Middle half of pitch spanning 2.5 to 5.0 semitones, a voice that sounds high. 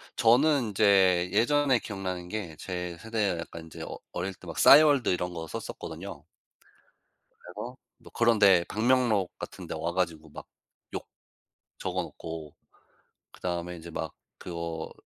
No: average, 4.7 semitones; very low, 95 Hz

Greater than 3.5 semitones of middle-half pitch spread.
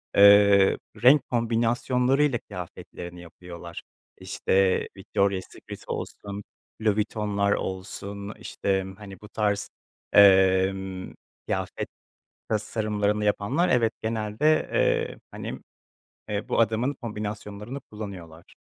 No: narrow, 2.5 semitones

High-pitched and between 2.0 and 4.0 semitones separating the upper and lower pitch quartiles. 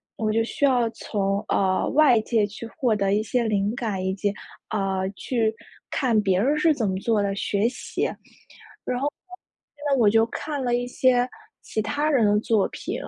Yes: high, 225 Hz; average, 3.7 semitones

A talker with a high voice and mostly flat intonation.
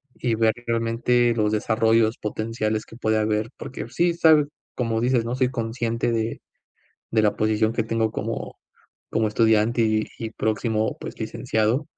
No: low, 115 Hz; narrow, 1.4 semitones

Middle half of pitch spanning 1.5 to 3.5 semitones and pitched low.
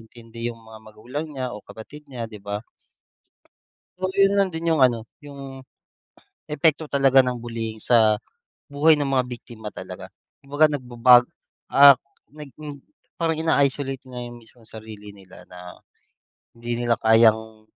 No: average, 4.2 semitones; low, 125 Hz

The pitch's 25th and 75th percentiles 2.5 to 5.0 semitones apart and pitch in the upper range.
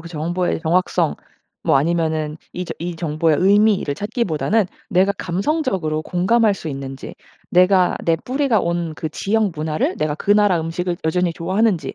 No: average, 4.0 semitones; medium, 175 Hz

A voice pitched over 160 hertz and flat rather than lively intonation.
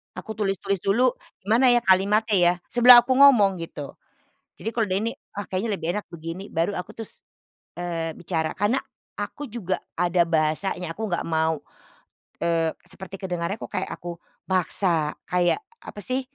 No: high, 190 Hz; average, 4.3 semitones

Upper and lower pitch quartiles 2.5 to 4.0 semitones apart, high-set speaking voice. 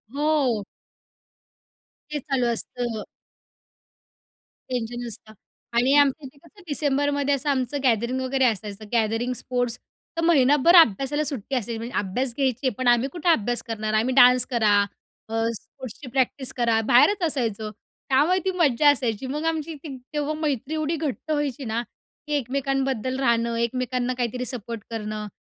Yes: average, 3.6 semitones; very high, 255 Hz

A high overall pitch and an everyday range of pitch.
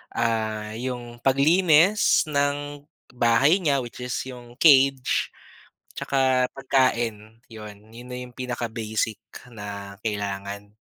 No: low, 120 Hz; average, 3.8 semitones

